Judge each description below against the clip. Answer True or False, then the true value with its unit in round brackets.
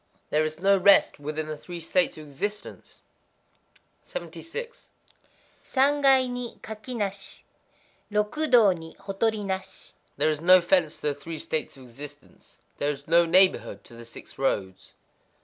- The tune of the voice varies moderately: False (5.8 semitones)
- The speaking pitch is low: False (185 Hz)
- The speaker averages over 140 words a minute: False (135 wpm)